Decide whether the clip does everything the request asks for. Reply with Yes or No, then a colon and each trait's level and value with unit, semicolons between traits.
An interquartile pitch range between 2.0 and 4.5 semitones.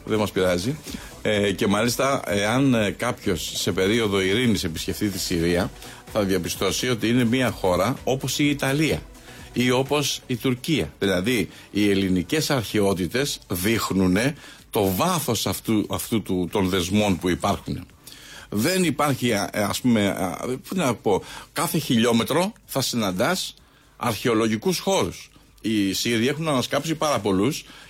No: wide, 5.4 semitones